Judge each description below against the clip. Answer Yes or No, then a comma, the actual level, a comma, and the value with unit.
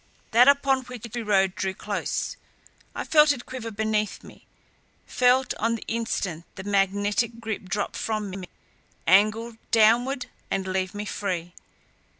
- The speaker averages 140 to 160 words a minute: Yes, average, 145 wpm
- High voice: Yes, high, 215 Hz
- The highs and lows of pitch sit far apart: No, average, 3.4 semitones